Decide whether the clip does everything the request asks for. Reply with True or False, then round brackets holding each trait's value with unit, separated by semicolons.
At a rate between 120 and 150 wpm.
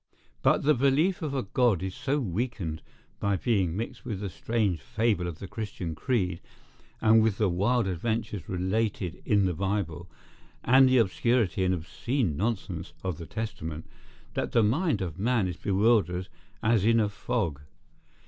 False (160 wpm)